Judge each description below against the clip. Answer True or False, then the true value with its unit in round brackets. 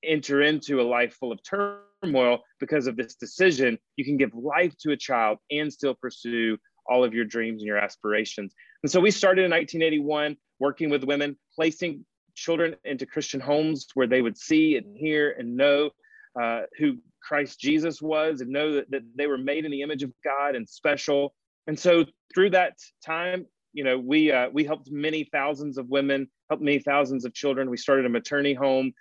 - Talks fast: False (195 wpm)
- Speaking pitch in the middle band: True (145 Hz)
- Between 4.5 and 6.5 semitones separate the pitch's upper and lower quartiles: False (3.2 semitones)